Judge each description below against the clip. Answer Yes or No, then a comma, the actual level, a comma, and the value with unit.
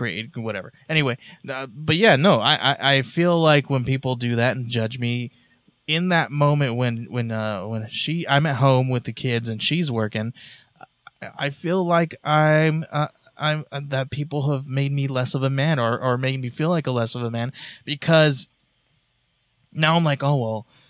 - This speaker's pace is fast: No, average, 195 wpm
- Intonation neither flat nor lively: Yes, average, 4.0 semitones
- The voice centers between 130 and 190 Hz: Yes, low, 135 Hz